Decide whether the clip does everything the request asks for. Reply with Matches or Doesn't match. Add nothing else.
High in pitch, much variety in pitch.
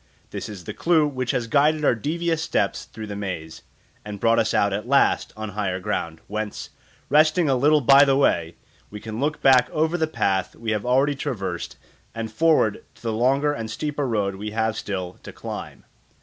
Doesn't match